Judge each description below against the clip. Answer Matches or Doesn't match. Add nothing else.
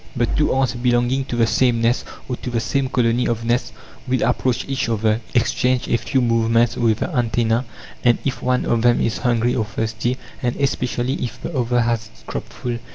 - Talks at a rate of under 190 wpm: Doesn't match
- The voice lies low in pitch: Matches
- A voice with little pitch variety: Matches